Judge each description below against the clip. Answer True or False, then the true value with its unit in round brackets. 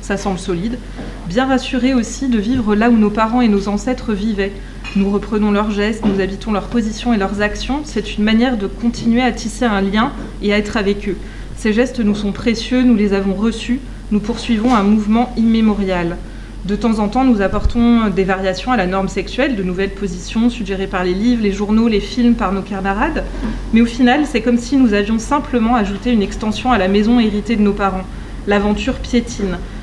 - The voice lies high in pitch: True (220 Hz)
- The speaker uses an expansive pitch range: False (3.1 semitones)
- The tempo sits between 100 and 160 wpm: False (205 wpm)